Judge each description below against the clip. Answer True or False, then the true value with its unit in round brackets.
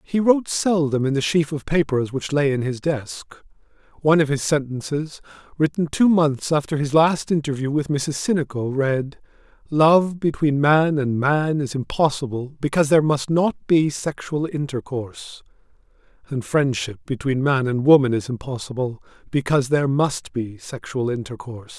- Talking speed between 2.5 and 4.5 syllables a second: False (4.9 syllables/s)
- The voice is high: False (140 Hz)